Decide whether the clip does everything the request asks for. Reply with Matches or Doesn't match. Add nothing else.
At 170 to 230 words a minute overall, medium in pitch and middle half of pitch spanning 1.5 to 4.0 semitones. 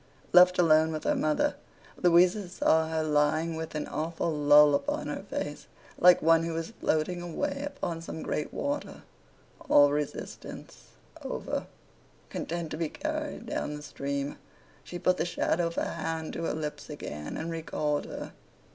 Doesn't match